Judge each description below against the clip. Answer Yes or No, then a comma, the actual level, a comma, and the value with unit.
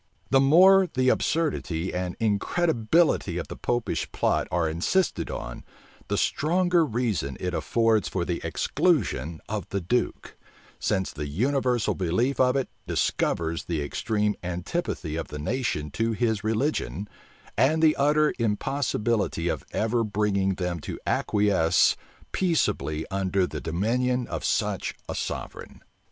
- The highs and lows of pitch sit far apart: Yes, wide, 7.2 semitones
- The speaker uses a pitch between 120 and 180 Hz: No, low, 105 Hz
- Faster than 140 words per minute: No, slow, 135 wpm